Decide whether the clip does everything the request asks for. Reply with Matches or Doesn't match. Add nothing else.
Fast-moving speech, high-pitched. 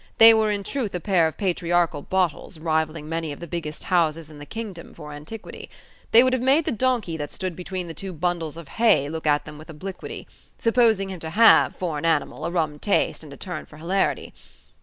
Doesn't match